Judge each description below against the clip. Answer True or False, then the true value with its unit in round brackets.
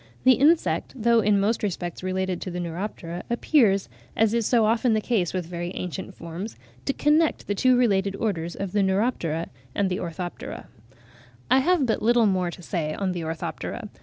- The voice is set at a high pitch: True (195 Hz)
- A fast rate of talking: False (180 wpm)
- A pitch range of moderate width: True (4.8 semitones)